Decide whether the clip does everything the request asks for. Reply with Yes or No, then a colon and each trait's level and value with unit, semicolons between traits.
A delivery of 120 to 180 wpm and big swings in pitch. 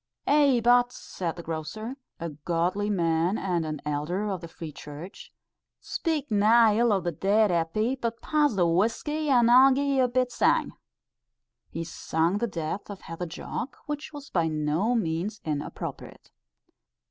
Yes: average, 160 wpm; wide, 6.6 semitones